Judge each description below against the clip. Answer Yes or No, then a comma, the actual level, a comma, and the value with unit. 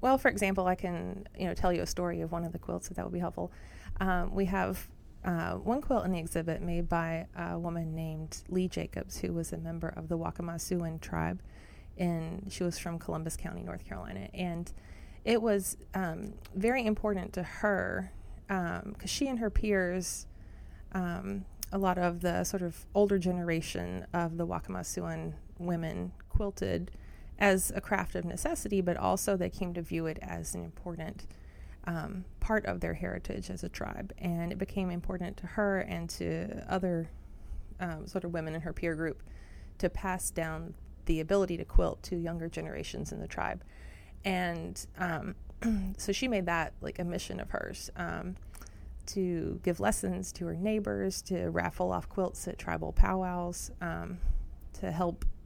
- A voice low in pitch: No, medium, 170 Hz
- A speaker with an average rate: Yes, average, 175 wpm